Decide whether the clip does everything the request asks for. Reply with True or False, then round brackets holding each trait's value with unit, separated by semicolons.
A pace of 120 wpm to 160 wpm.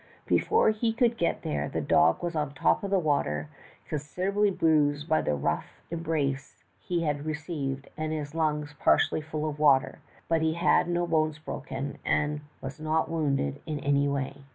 False (180 wpm)